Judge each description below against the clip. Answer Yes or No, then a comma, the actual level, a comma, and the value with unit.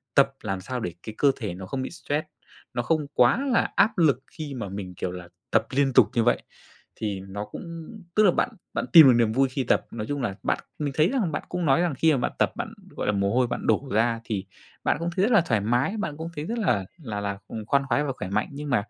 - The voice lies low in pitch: Yes, low, 130 Hz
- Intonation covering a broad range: Yes, wide, 6.6 semitones